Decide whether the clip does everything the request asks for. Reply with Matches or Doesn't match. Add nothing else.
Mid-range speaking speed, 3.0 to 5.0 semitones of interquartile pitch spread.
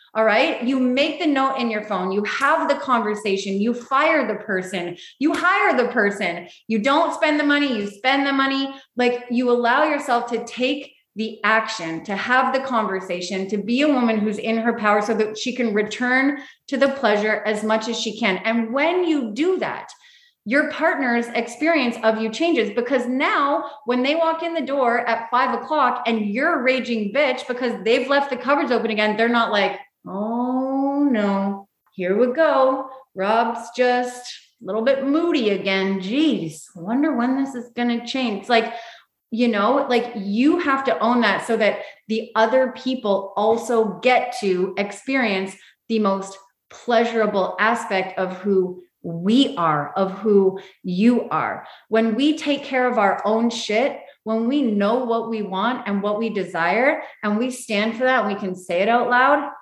Matches